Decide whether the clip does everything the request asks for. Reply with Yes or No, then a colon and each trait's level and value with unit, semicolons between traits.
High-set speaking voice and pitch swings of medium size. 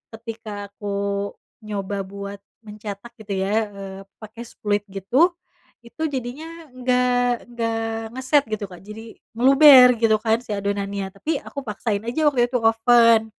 Yes: high, 225 Hz; average, 3.6 semitones